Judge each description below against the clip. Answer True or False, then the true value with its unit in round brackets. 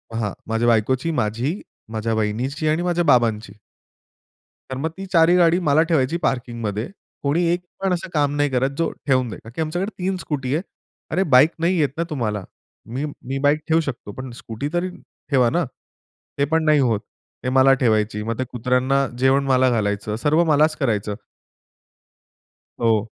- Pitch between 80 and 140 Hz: True (135 Hz)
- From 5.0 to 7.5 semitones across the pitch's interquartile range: True (5.4 semitones)